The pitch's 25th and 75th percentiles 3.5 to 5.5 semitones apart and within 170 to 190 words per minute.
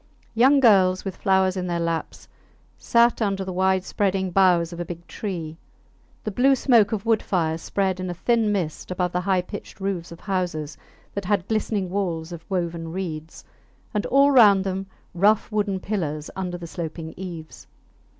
No: average, 2.9 semitones; average, 175 wpm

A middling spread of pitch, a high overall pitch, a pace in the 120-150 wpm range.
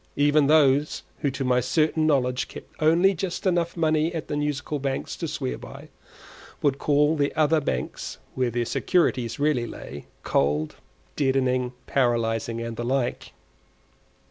No: average, 4.0 semitones; medium, 140 Hz; average, 145 wpm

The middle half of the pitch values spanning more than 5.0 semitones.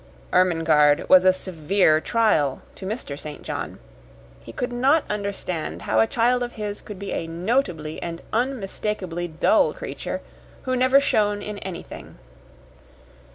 Yes: wide, 5.6 semitones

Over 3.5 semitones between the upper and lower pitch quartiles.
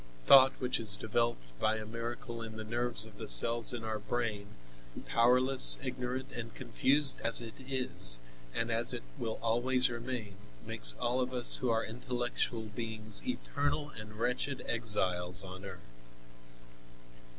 No: narrow, 2.6 semitones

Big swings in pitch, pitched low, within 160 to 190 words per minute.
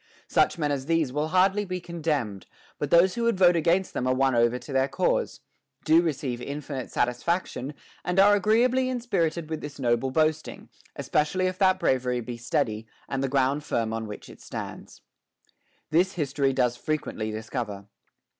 No: wide, 5.8 semitones; medium, 150 Hz; average, 175 wpm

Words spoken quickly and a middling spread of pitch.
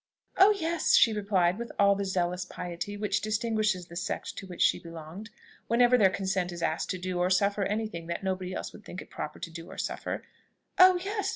Yes: fast, 215 wpm; average, 3.4 semitones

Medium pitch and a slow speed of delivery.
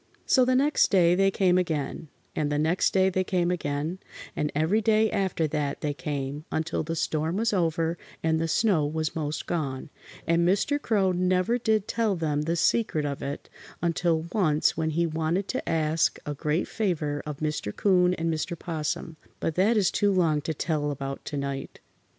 No: medium, 165 Hz; average, 185 wpm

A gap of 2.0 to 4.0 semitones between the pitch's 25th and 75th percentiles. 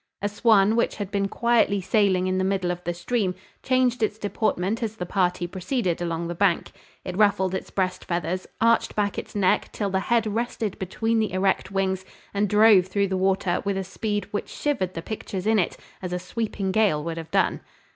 Yes: average, 2.9 semitones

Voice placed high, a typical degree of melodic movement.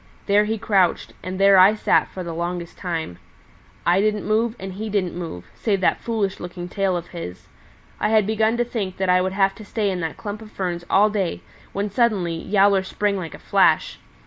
Yes: high, 195 Hz; average, 3.0 semitones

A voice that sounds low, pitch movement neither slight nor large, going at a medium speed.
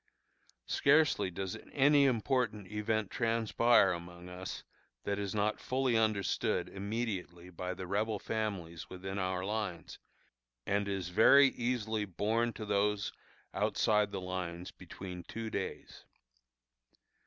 No: low, 105 Hz; average, 3.3 semitones; slow, 120 wpm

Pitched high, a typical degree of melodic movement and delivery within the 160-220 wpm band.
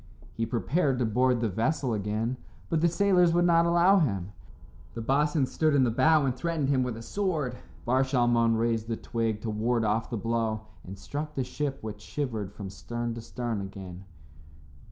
No: low, 120 Hz; average, 4.9 semitones; average, 190 wpm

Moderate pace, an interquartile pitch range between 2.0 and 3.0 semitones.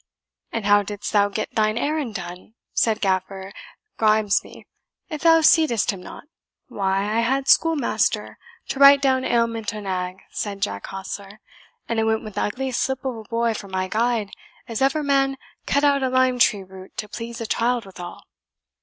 No: average, 180 wpm; average, 4.6 semitones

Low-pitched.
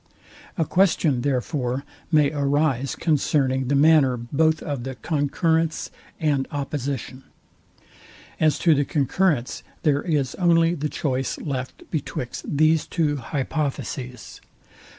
No: medium, 145 Hz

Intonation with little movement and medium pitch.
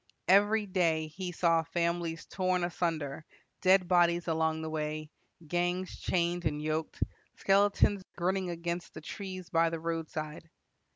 Yes: narrow, 2.3 semitones; medium, 170 Hz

